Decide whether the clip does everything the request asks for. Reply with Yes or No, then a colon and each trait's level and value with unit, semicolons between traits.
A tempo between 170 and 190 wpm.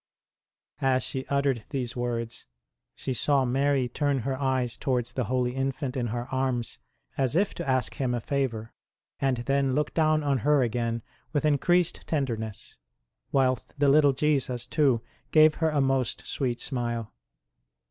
No: average, 155 wpm